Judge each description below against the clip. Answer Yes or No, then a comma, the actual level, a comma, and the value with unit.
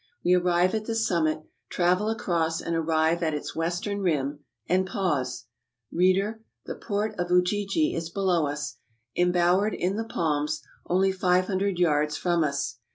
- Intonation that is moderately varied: Yes, average, 3.2 semitones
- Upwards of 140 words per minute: Yes, average, 165 wpm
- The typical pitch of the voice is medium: Yes, medium, 180 Hz